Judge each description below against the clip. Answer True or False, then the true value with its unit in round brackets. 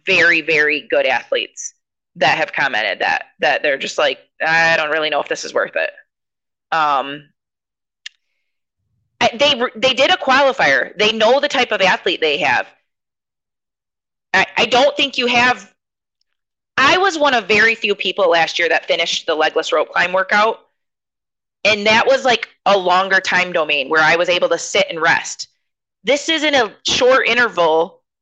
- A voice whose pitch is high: True (215 Hz)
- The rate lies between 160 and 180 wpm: True (165 wpm)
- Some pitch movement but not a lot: False (7.9 semitones)